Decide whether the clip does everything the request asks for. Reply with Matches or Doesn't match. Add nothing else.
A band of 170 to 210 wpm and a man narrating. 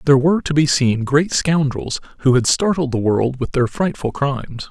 Matches